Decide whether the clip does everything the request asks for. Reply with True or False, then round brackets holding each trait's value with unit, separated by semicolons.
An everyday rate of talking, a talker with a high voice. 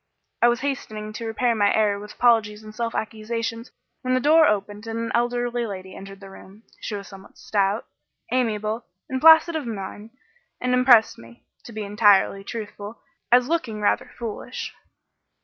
True (165 wpm; 220 Hz)